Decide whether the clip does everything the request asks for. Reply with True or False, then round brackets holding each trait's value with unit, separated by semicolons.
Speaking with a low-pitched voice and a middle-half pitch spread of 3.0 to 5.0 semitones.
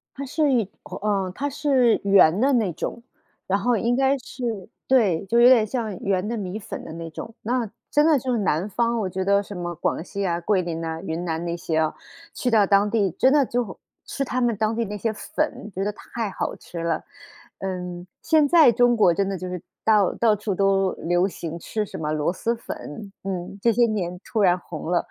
False (200 Hz; 4.7 semitones)